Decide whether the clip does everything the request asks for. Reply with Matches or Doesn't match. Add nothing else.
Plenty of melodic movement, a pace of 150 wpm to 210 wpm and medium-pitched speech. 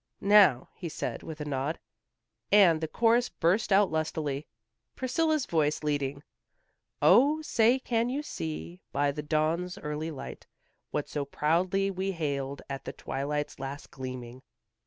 Doesn't match